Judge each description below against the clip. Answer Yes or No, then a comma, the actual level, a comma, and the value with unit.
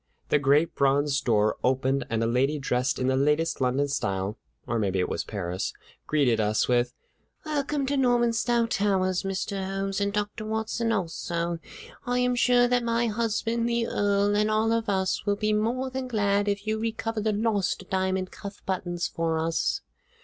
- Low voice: No, high, 195 Hz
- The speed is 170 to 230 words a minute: Yes, average, 175 wpm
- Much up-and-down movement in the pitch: Yes, wide, 8.0 semitones